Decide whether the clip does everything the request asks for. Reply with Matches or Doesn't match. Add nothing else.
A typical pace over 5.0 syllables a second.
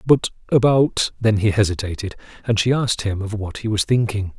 Matches